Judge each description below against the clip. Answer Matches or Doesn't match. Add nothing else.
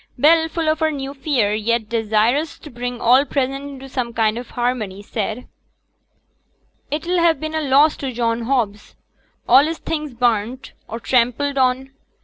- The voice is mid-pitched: Doesn't match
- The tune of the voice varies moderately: Matches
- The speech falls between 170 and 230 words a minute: Doesn't match